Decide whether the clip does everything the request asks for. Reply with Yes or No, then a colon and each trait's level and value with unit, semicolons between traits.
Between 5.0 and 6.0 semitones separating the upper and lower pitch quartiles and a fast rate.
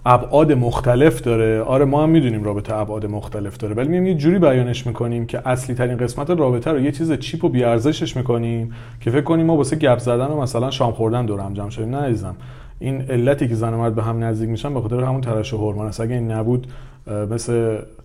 No: average, 3.6 semitones; fast, 215 wpm